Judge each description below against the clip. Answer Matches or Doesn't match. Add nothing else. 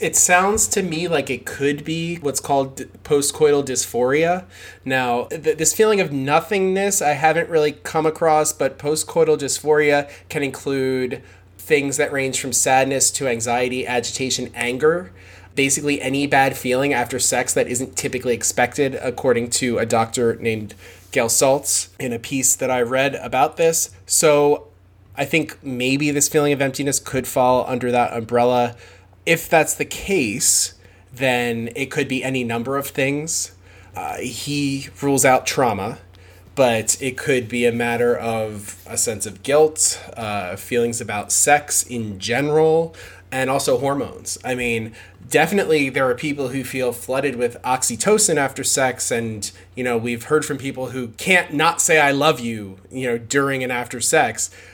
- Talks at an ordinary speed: Matches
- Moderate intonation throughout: Matches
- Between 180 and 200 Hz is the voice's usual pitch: Doesn't match